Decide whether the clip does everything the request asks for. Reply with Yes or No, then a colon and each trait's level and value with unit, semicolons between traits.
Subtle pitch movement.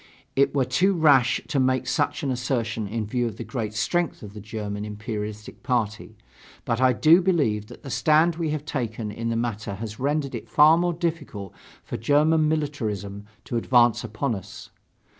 No: wide, 5.6 semitones